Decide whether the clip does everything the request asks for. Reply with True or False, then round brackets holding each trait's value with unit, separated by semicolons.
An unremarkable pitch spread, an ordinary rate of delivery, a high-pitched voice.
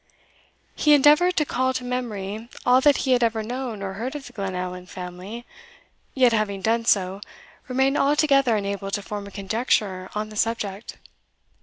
True (4.5 semitones; 165 wpm; 225 Hz)